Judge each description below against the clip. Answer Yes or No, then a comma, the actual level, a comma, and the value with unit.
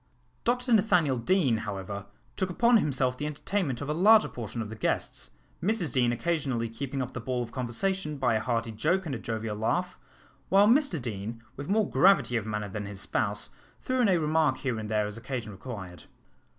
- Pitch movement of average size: No, wide, 8.0 semitones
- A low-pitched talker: Yes, low, 130 Hz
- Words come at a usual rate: Yes, average, 195 wpm